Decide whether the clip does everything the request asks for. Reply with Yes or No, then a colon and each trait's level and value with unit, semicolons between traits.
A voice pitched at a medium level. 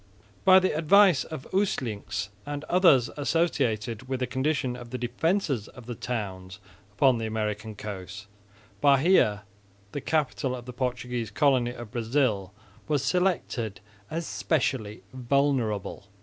No: low, 125 Hz